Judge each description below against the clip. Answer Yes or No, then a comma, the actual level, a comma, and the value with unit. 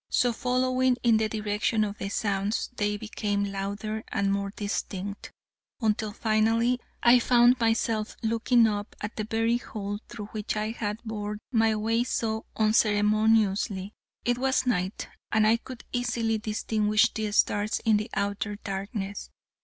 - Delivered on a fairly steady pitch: Yes, narrow, 1.7 semitones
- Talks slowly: No, average, 145 wpm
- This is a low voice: No, high, 215 Hz